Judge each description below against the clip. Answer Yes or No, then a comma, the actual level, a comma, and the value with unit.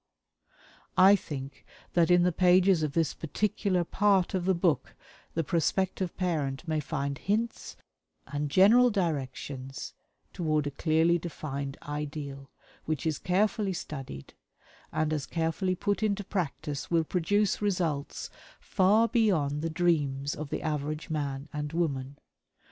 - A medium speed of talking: No, slow, 130 wpm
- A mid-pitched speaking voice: Yes, medium, 160 Hz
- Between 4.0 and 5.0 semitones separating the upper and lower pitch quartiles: Yes, average, 4.3 semitones